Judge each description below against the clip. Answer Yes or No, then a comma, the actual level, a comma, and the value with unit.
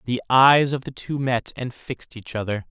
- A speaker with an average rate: No, fast, 220 wpm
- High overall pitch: No, low, 125 Hz